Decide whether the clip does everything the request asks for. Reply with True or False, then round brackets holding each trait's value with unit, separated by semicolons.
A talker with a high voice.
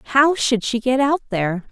True (245 Hz)